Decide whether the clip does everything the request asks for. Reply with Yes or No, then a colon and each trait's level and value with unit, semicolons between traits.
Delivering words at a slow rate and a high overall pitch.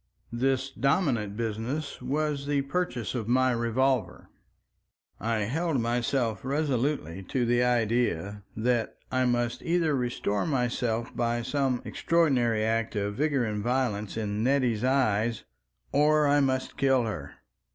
No: slow, 130 wpm; low, 125 Hz